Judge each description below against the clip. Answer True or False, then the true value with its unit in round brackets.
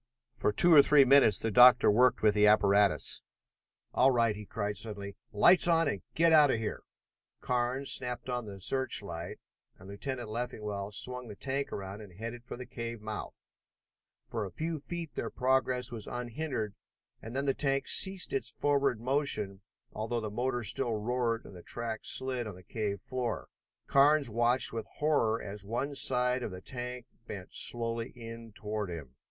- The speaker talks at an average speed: True (175 wpm)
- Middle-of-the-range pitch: False (120 Hz)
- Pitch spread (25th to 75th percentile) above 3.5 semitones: True (3.9 semitones)